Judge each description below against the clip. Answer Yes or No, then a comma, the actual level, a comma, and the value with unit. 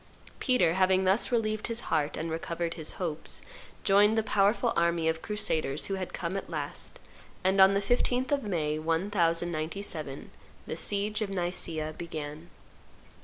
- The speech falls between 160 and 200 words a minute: No, average, 150 wpm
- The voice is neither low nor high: Yes, medium, 180 Hz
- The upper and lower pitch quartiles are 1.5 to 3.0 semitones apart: No, average, 3.9 semitones